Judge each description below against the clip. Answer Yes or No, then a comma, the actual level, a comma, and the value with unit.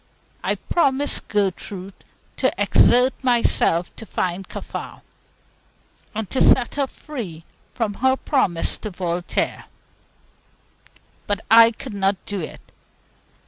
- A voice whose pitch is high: Yes, high, 210 Hz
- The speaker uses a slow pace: Yes, slow, 105 wpm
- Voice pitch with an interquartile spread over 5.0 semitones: Yes, wide, 5.5 semitones